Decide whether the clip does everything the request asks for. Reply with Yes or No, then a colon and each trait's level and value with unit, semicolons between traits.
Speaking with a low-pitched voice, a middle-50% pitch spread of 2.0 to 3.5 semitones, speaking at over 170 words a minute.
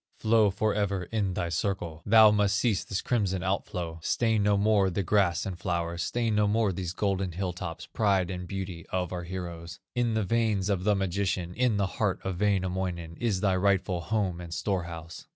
Yes: very low, 95 Hz; average, 2.8 semitones; average, 190 wpm